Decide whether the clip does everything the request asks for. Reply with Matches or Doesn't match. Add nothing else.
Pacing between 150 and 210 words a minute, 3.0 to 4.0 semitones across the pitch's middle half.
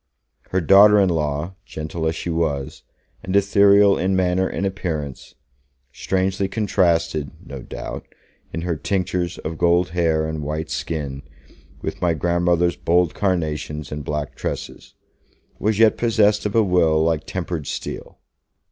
Doesn't match